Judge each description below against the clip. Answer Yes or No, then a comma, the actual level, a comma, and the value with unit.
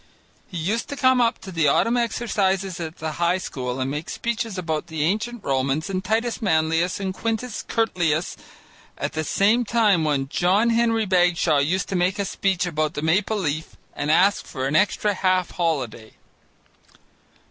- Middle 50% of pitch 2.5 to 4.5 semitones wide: No, average, 5.2 semitones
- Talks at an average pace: Yes, average, 170 wpm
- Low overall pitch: No, medium, 180 Hz